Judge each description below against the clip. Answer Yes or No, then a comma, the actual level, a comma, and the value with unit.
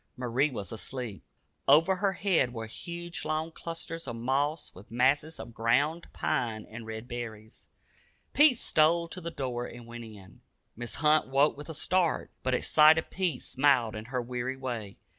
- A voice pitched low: Yes, low, 130 Hz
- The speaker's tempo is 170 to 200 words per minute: Yes, average, 175 wpm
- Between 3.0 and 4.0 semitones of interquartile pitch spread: No, average, 5.3 semitones